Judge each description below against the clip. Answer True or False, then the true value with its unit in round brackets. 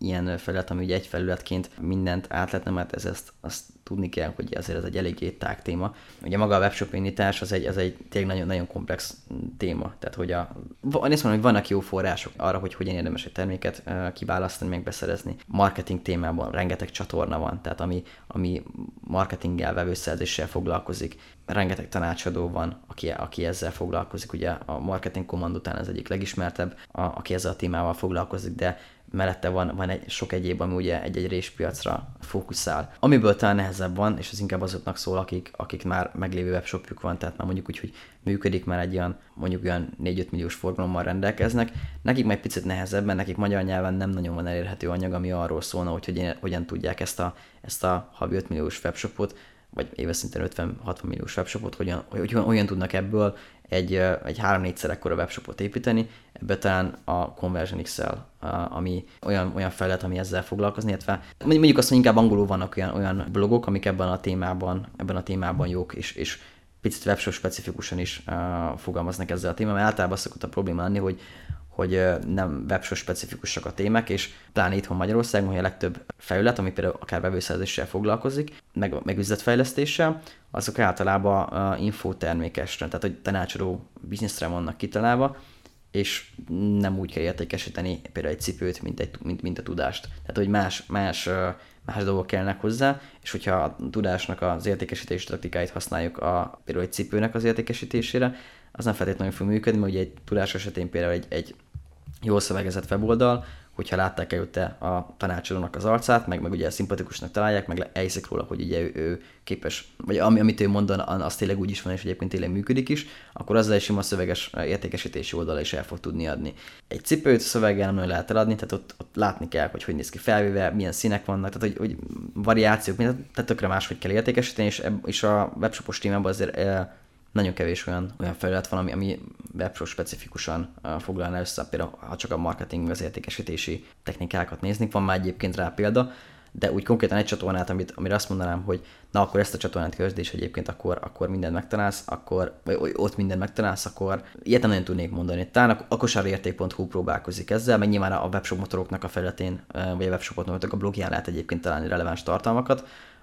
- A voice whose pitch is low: True (95 Hz)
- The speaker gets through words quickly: True (180 wpm)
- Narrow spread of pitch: True (2.3 semitones)